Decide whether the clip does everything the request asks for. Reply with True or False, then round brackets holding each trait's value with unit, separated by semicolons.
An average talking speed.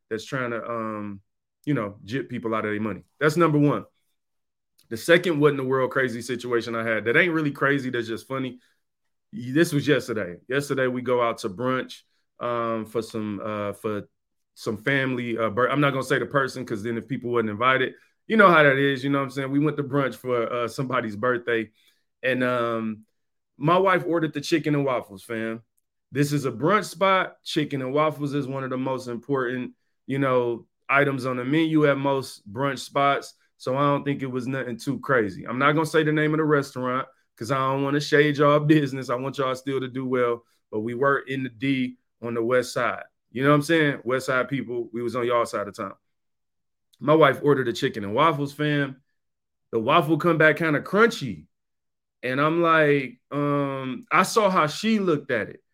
False (215 wpm)